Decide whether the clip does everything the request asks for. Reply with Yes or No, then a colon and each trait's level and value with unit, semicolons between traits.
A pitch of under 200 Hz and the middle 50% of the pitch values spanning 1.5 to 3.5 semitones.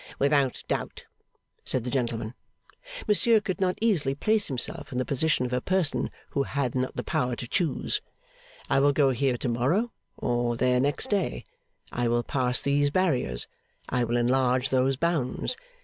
No: low, 135 Hz; average, 4.0 semitones